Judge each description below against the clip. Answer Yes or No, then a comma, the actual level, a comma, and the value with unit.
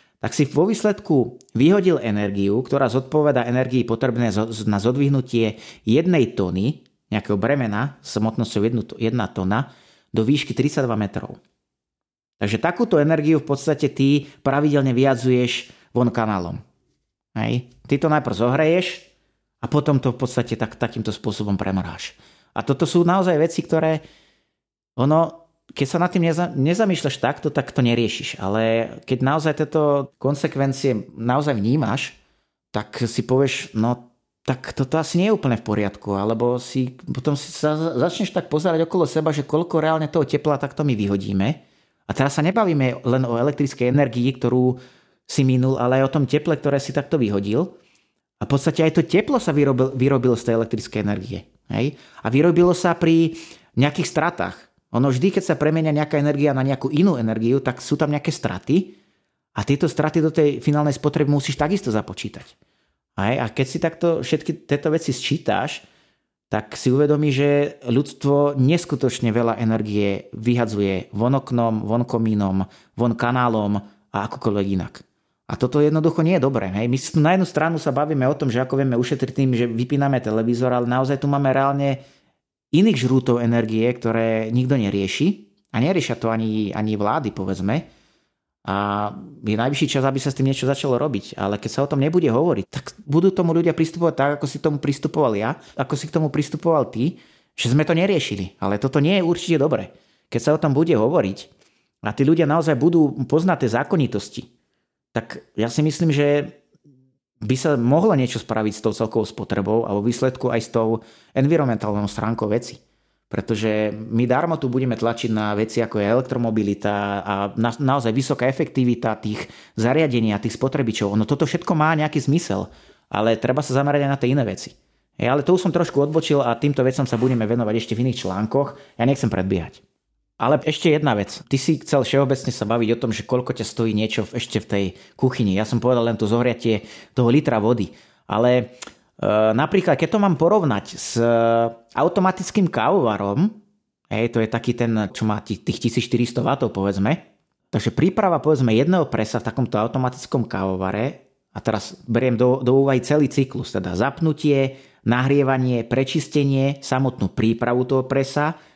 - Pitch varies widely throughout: No, average, 4.9 semitones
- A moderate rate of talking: No, fast, 170 wpm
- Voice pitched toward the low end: Yes, low, 130 Hz